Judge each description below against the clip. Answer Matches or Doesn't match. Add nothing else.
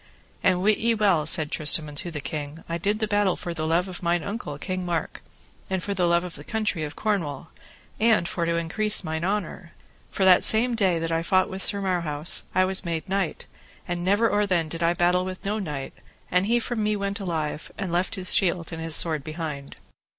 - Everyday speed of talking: Doesn't match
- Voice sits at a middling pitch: Matches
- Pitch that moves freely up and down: Doesn't match